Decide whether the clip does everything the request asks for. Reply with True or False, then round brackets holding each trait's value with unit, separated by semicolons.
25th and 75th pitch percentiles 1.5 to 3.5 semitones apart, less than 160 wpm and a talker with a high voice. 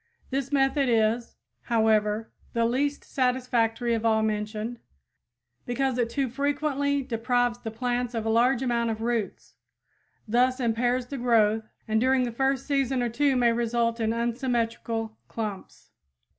True (2.4 semitones; 145 wpm; 240 Hz)